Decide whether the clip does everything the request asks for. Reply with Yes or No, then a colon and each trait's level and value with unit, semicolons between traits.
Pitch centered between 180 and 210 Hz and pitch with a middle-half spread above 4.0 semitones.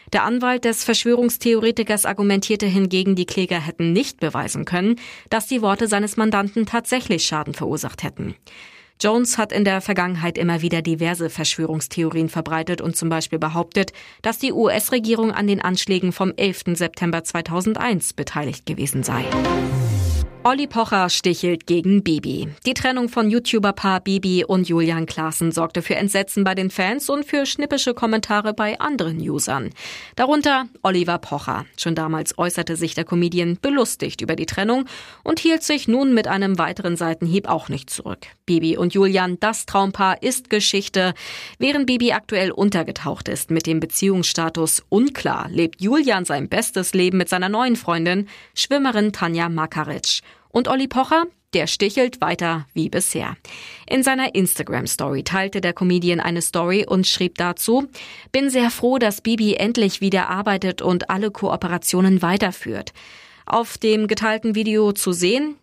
Yes: high, 190 Hz; average, 4.9 semitones